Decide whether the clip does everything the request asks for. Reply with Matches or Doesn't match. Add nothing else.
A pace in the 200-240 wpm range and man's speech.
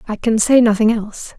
Doesn't match